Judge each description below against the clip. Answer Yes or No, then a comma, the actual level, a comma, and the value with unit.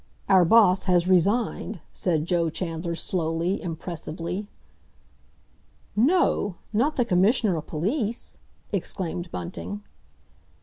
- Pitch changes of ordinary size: Yes, average, 3.9 semitones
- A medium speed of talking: No, slow, 95 wpm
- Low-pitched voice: No, medium, 180 Hz